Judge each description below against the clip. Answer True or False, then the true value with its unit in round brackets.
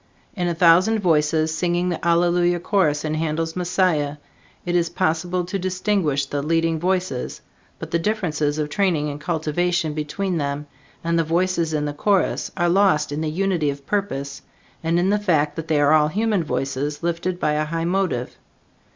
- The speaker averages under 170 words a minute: False (175 wpm)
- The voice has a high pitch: False (165 Hz)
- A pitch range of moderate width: True (3.1 semitones)